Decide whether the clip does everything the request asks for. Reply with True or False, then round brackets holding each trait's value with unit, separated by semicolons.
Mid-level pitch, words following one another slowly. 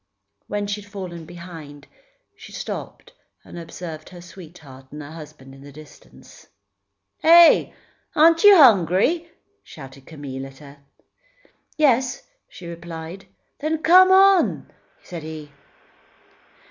True (170 Hz; 115 wpm)